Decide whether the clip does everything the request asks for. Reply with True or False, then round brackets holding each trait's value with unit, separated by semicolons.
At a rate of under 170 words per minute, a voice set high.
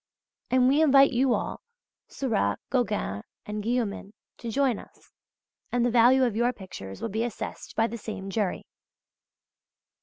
True (150 wpm; 230 Hz)